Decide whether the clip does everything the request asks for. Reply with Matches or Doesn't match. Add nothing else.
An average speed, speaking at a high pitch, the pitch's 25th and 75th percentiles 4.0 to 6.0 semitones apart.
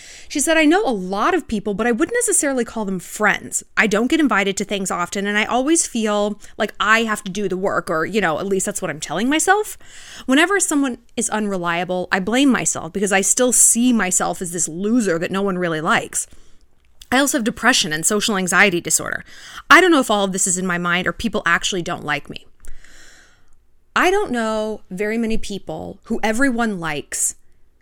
Doesn't match